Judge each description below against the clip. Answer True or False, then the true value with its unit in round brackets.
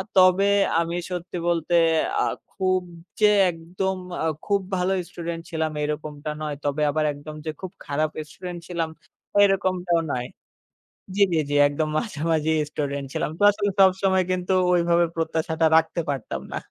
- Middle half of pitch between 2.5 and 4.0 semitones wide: True (3.1 semitones)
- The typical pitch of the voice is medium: True (170 Hz)